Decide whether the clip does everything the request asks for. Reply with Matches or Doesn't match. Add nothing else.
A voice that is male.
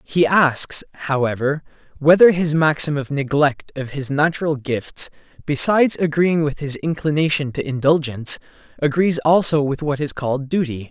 Matches